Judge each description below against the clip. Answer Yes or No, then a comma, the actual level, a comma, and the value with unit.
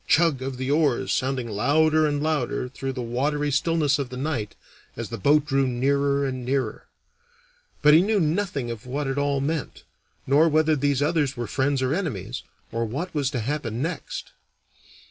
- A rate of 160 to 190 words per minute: Yes, average, 180 wpm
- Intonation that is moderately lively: Yes, average, 3.0 semitones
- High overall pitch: No, medium, 140 Hz